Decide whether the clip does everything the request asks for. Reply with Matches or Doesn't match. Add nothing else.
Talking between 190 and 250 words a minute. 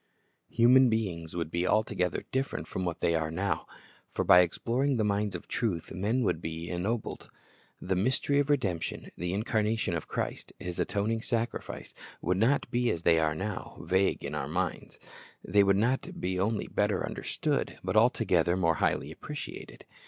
Doesn't match